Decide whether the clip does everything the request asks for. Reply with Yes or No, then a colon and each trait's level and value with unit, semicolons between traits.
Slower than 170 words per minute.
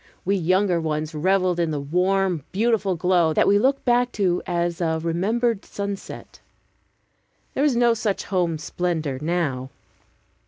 Yes: average, 150 wpm